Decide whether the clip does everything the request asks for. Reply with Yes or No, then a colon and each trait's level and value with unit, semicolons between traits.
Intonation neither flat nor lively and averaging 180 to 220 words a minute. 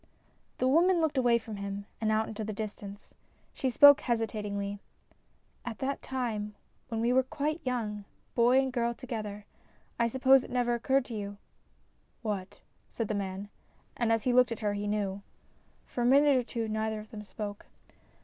Yes: average, 3.4 semitones; average, 190 wpm